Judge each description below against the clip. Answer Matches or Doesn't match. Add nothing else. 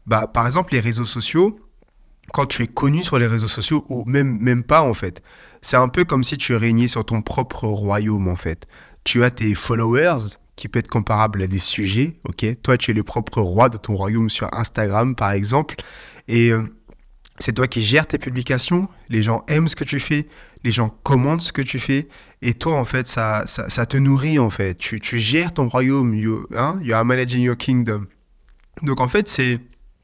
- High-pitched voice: Doesn't match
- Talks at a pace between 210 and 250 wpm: Matches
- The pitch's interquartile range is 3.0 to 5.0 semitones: Matches